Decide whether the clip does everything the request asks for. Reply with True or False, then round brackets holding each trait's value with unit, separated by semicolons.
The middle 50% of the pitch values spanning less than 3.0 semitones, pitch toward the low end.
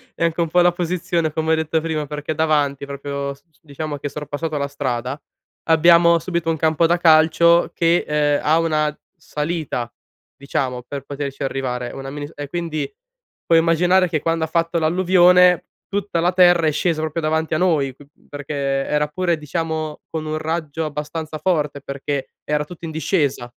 False (2.6 semitones; 155 Hz)